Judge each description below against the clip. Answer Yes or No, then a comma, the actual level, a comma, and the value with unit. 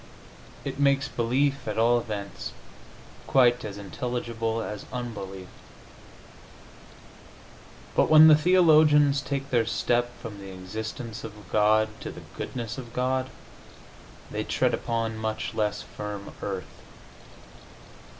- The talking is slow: Yes, slow, 115 wpm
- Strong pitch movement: No, average, 3.8 semitones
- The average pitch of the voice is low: Yes, low, 115 Hz